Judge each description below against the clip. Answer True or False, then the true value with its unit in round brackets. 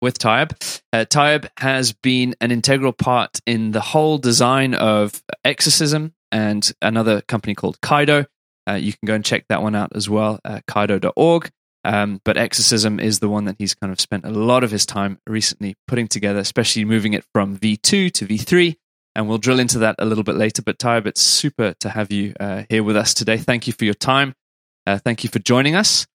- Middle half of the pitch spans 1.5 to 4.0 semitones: True (3.5 semitones)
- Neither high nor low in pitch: False (110 Hz)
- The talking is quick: True (210 wpm)